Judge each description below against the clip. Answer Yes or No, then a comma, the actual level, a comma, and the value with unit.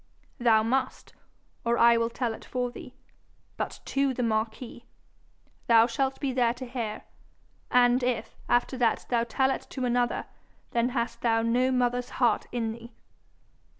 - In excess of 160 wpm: No, average, 155 wpm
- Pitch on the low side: No, high, 240 Hz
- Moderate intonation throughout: No, narrow, 1.4 semitones